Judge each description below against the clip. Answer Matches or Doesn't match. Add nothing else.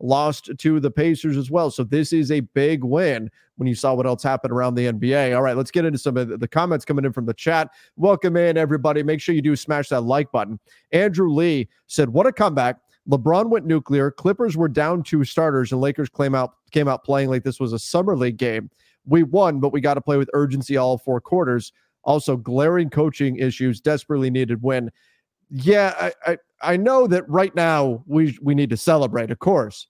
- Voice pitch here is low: Doesn't match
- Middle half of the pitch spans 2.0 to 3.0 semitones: Doesn't match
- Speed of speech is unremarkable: Doesn't match